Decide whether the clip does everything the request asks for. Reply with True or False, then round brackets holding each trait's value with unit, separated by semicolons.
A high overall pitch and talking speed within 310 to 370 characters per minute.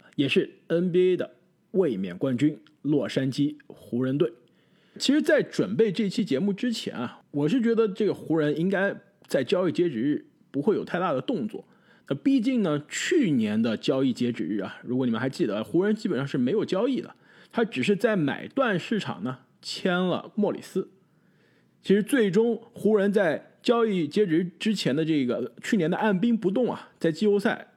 False (195 Hz; 270 characters per minute)